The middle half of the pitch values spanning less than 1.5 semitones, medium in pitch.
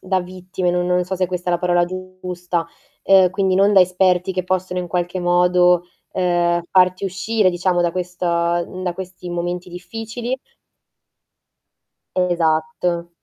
Yes: narrow, 0.9 semitones; medium, 180 Hz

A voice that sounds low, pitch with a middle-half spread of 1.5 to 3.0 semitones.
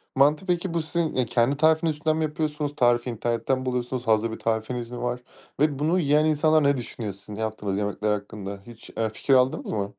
No: low, 125 Hz; average, 5.3 semitones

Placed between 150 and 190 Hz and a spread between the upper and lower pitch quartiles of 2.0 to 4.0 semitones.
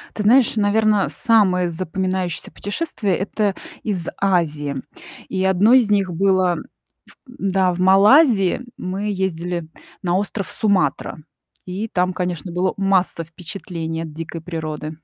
Yes: medium, 185 Hz; average, 2.7 semitones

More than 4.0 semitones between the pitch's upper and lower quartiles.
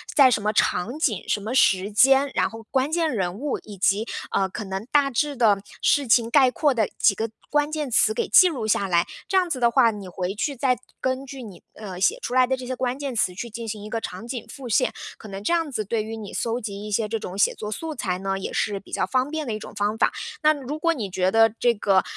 Yes: average, 4.8 semitones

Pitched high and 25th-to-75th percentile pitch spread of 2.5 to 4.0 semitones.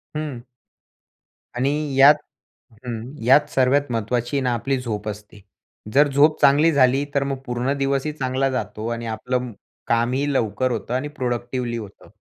No: low, 125 Hz; average, 2.8 semitones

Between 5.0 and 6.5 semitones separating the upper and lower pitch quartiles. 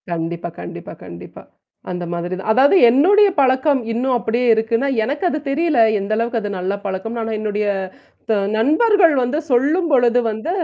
Yes: wide, 5.4 semitones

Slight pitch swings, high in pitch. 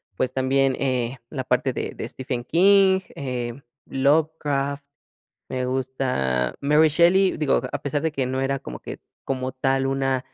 No: narrow, 2.2 semitones; low, 135 Hz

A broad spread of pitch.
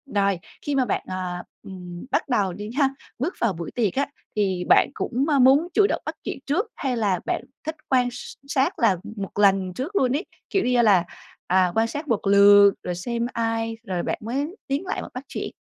Yes: wide, 5.8 semitones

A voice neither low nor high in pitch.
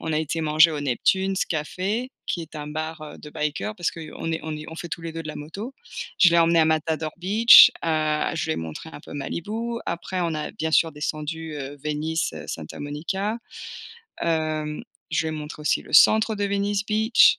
Yes: medium, 160 Hz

